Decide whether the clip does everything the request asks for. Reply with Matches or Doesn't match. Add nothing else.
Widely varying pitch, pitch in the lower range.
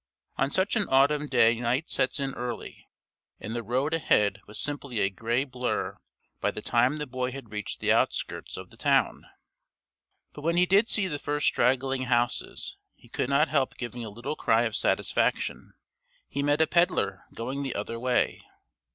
Doesn't match